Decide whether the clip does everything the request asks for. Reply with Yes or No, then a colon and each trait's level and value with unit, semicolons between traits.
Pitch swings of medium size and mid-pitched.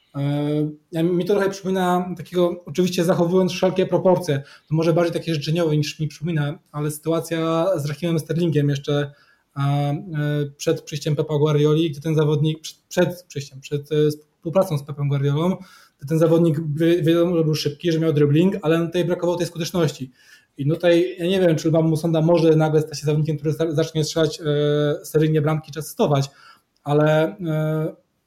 No: narrow, 2.2 semitones; medium, 160 Hz